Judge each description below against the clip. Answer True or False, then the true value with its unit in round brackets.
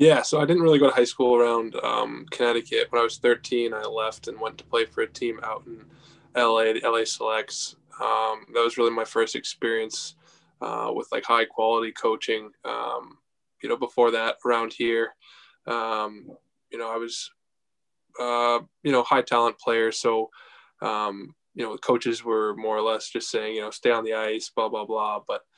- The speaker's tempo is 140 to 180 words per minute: False (195 wpm)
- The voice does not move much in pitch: True (2.0 semitones)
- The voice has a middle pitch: False (115 Hz)